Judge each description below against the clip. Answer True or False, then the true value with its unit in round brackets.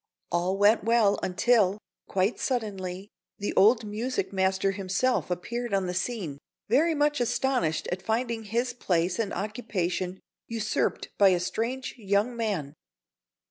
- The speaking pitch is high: True (205 Hz)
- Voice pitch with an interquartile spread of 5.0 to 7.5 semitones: False (4.0 semitones)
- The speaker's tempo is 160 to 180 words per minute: False (135 wpm)